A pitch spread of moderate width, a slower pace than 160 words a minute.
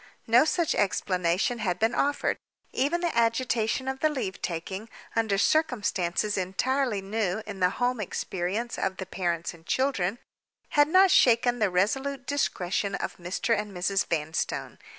No: wide, 5.7 semitones; average, 150 wpm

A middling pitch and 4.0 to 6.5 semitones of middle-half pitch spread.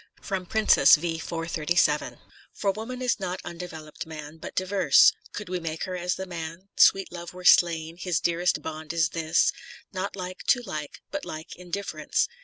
No: medium, 175 Hz; narrow, 2.6 semitones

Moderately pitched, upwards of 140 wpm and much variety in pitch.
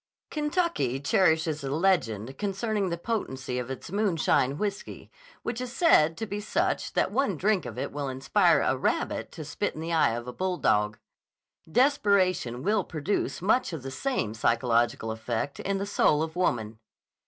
Yes: medium, 165 Hz; average, 165 wpm; wide, 7.9 semitones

